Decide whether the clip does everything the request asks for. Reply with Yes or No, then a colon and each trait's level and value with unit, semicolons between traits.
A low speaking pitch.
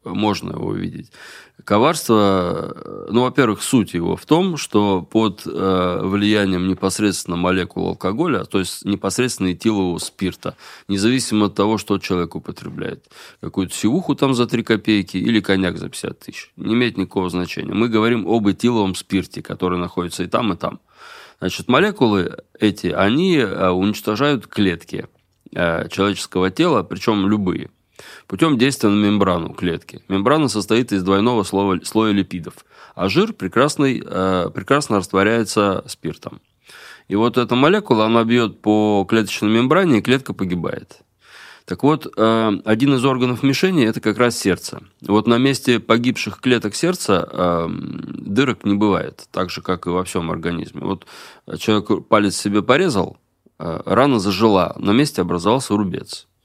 Yes: low, 105 Hz